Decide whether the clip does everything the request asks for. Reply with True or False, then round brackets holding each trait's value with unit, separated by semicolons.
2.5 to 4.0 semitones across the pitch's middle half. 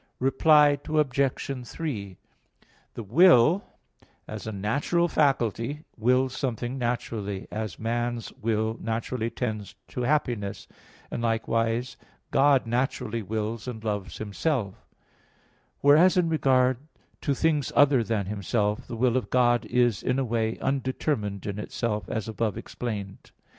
True (3.6 semitones)